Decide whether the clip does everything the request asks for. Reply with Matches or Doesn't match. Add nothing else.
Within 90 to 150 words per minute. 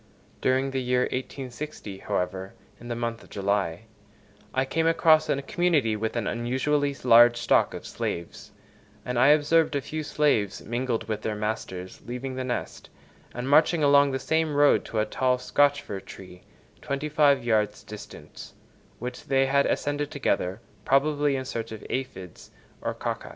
Doesn't match